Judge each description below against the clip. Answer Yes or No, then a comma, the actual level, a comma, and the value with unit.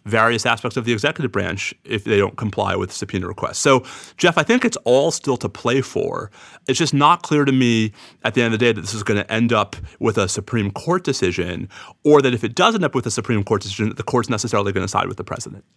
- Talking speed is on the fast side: Yes, fast, 265 wpm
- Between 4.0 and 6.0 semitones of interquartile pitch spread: Yes, average, 4.4 semitones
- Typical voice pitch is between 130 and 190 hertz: No, low, 115 Hz